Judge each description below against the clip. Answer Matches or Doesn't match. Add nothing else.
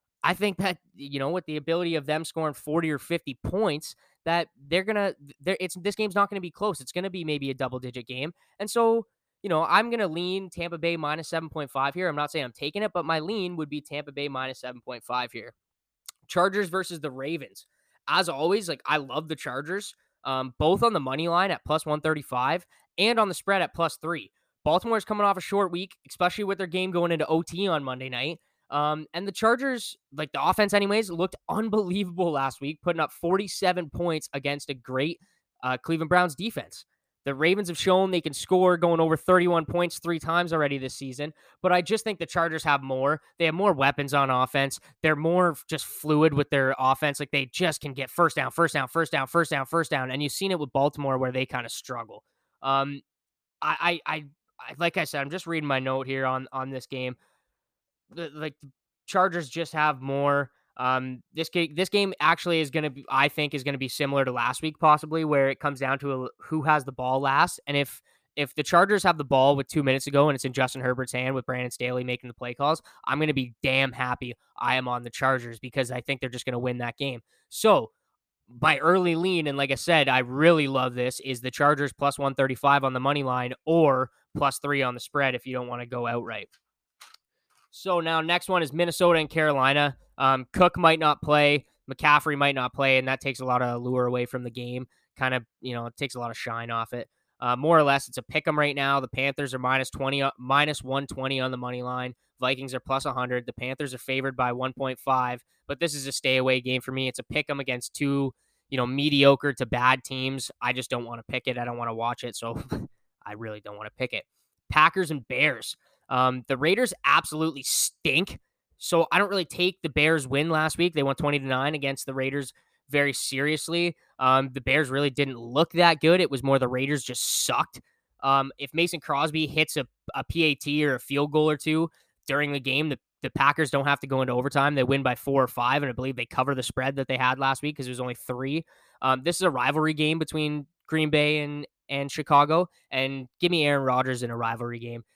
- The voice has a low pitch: Doesn't match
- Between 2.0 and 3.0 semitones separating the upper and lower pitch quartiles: Doesn't match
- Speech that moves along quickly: Matches